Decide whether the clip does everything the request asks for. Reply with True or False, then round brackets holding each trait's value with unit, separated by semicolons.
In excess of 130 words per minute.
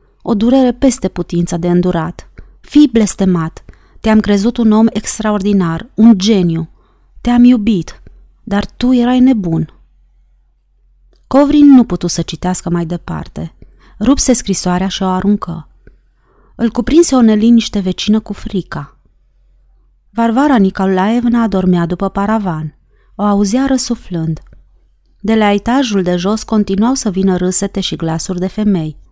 False (125 wpm)